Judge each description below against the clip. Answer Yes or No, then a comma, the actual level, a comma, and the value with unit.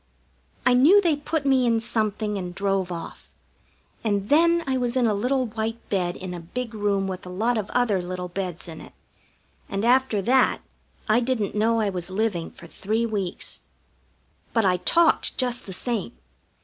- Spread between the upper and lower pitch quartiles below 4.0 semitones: No, average, 4.6 semitones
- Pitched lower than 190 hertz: No, high, 215 Hz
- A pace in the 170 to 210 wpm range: Yes, average, 180 wpm